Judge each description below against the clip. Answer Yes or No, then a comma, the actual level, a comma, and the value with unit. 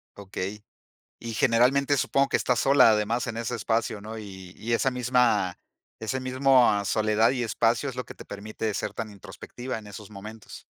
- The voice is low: Yes, low, 115 Hz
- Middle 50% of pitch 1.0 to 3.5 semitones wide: Yes, average, 2.9 semitones